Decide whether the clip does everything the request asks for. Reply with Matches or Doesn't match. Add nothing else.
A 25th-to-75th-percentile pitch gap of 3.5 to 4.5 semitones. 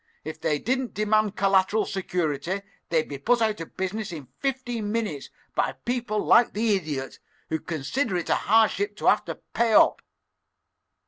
Doesn't match